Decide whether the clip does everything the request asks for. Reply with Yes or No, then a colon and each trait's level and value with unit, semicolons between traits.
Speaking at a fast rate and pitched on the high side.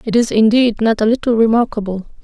No: average, 190 wpm; high, 225 Hz